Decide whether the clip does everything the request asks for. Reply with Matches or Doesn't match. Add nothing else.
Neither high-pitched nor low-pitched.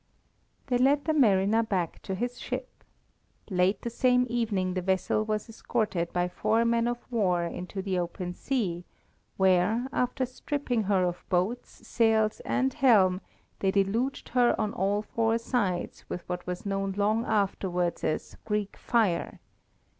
Doesn't match